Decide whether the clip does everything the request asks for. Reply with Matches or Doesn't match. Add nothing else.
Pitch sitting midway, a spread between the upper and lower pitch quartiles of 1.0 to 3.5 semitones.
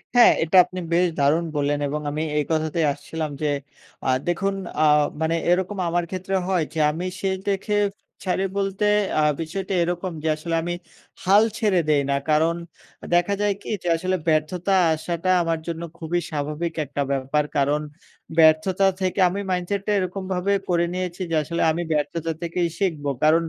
Matches